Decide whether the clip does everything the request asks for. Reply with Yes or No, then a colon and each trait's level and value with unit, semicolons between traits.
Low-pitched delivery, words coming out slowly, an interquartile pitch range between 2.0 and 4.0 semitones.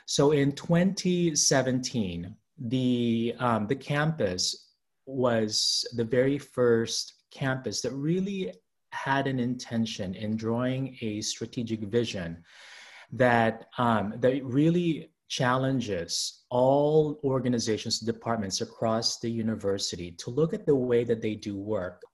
Yes: low, 120 Hz; slow, 115 wpm; average, 3.4 semitones